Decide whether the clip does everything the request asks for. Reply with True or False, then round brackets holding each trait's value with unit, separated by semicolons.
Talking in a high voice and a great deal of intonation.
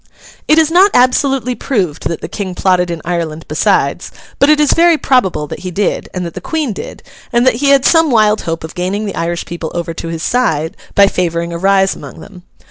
True (195 Hz; 7.2 semitones)